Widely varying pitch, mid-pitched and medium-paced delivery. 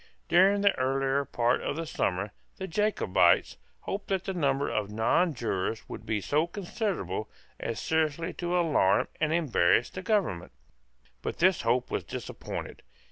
Yes: wide, 8.2 semitones; medium, 145 Hz; average, 145 wpm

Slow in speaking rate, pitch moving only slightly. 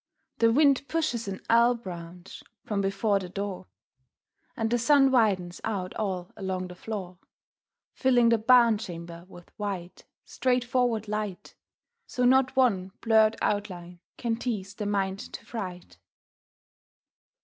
No: slow, 130 wpm; average, 4.2 semitones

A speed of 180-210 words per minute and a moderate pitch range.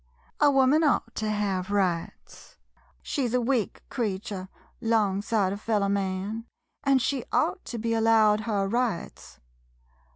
No: average, 155 wpm; average, 3.4 semitones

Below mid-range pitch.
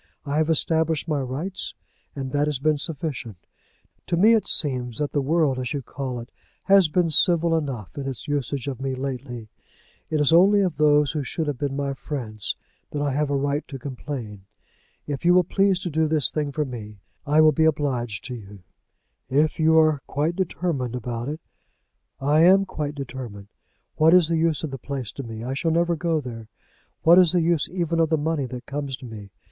No: medium, 145 Hz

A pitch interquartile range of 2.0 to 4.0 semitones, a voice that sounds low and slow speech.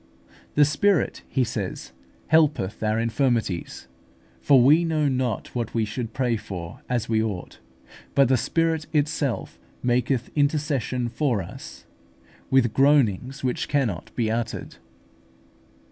No: average, 4.4 semitones; low, 125 Hz; slow, 125 wpm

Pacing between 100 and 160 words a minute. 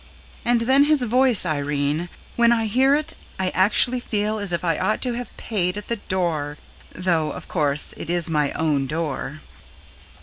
No: average, 175 wpm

